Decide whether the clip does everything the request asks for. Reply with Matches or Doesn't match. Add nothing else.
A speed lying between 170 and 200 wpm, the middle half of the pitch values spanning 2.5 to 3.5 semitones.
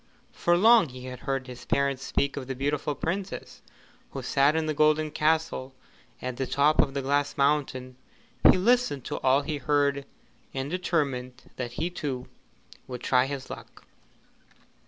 Doesn't match